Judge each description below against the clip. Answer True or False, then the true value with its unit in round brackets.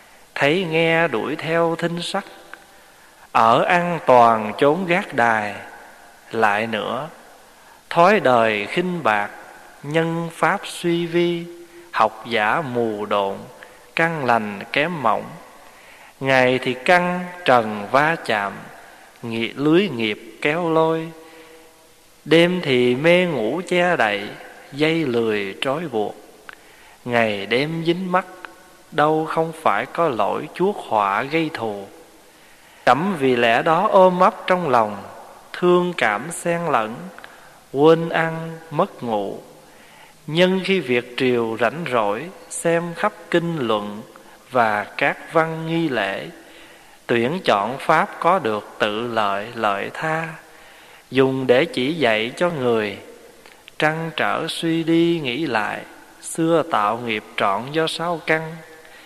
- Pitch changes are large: True (6.2 semitones)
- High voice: False (160 Hz)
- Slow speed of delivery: True (125 wpm)